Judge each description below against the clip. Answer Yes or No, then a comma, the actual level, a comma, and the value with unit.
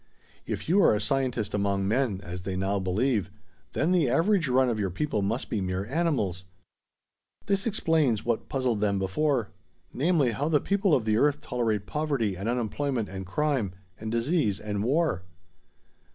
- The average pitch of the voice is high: No, low, 120 Hz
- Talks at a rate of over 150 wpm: Yes, average, 170 wpm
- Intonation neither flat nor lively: No, wide, 6.7 semitones